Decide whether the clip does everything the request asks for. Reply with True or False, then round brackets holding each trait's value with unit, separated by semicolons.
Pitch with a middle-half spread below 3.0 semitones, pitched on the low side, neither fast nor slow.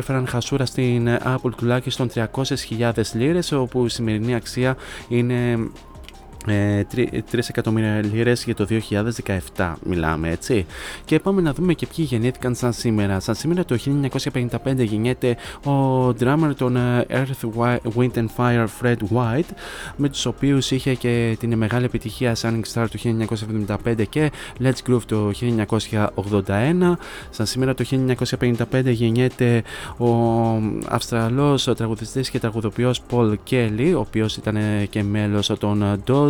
True (2.6 semitones; 120 Hz; 130 wpm)